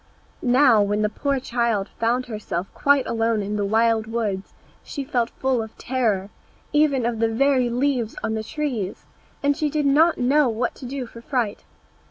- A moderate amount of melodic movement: Yes, average, 3.8 semitones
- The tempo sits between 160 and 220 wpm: Yes, average, 180 wpm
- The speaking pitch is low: No, high, 235 Hz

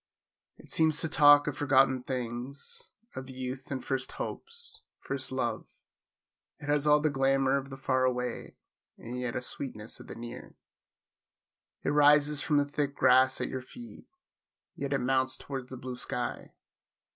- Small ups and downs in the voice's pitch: Yes, narrow, 2.2 semitones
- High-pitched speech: No, low, 135 Hz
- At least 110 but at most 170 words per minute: Yes, average, 160 wpm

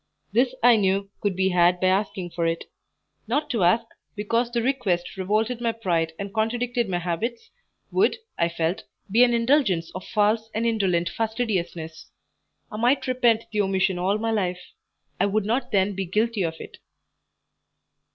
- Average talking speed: Yes, average, 165 wpm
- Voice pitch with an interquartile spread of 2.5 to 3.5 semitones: No, average, 4.2 semitones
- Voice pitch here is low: No, high, 210 Hz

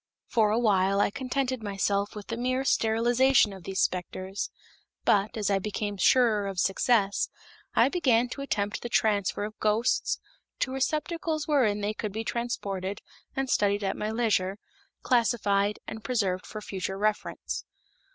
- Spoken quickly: No, average, 150 wpm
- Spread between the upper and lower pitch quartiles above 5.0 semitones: No, average, 3.4 semitones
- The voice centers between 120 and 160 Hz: No, high, 215 Hz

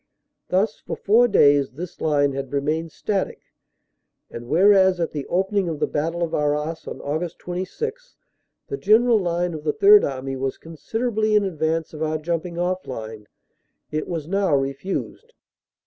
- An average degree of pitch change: Yes, average, 4.9 semitones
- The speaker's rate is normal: Yes, average, 160 wpm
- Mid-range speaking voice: Yes, medium, 165 Hz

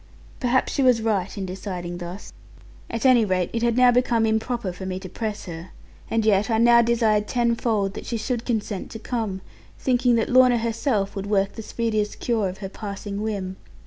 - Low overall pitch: No, high, 220 Hz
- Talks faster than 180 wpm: Yes, average, 195 wpm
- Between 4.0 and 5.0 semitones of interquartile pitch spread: No, average, 3.3 semitones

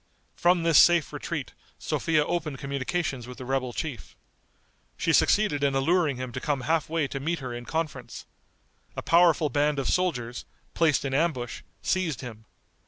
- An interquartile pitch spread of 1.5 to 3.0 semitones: No, average, 4.2 semitones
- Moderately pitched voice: Yes, medium, 145 Hz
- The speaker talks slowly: No, average, 165 wpm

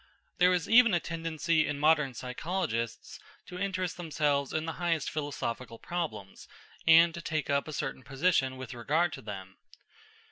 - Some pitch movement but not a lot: Yes, average, 4.6 semitones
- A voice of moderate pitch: Yes, medium, 155 Hz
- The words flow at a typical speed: Yes, average, 155 wpm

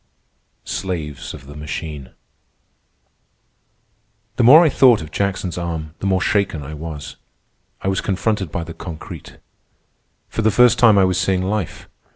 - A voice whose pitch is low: Yes, very low, 95 Hz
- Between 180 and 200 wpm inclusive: No, average, 150 wpm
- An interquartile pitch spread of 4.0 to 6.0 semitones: Yes, average, 4.5 semitones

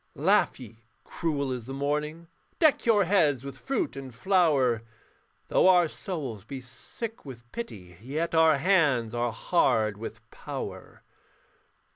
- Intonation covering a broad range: Yes, wide, 6.4 semitones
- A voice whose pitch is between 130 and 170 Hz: Yes, medium, 140 Hz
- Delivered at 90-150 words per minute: Yes, slow, 135 wpm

